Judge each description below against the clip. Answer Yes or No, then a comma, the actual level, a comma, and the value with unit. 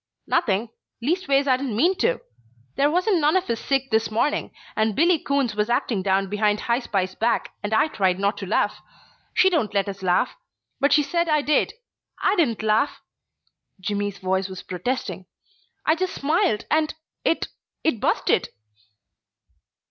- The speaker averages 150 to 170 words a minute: Yes, average, 165 wpm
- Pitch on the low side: No, high, 235 Hz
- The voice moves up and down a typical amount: No, wide, 6.9 semitones